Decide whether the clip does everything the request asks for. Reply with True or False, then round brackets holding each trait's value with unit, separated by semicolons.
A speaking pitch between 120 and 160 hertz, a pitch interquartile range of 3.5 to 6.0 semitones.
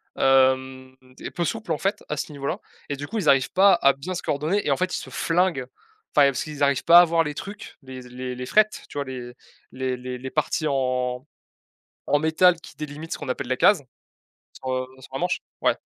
True (140 Hz; 4.5 semitones)